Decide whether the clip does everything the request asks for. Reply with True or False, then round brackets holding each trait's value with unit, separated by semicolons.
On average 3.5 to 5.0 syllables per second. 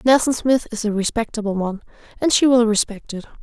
False (5.7 syllables/s)